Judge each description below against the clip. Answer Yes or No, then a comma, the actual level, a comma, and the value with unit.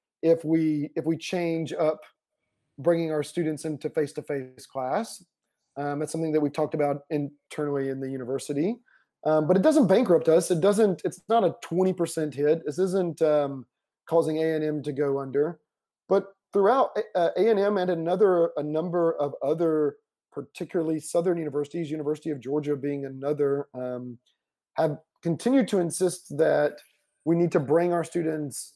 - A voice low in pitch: No, medium, 160 Hz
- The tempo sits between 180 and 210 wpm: No, average, 155 wpm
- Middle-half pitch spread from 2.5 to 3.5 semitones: Yes, average, 2.8 semitones